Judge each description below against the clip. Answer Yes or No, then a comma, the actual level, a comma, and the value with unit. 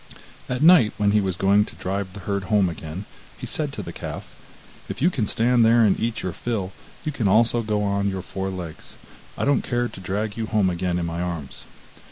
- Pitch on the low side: Yes, low, 100 Hz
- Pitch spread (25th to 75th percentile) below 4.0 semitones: Yes, average, 3.6 semitones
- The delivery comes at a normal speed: No, fast, 225 wpm